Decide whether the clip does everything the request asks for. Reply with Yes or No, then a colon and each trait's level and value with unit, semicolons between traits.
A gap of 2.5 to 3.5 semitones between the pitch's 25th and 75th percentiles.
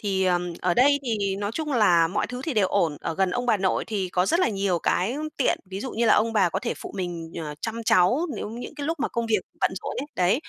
No: average, 5.1 semitones